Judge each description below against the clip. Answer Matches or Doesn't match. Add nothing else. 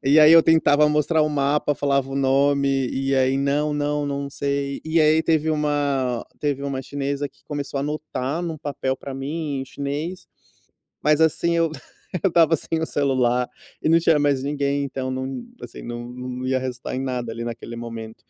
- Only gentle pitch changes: Matches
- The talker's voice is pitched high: Doesn't match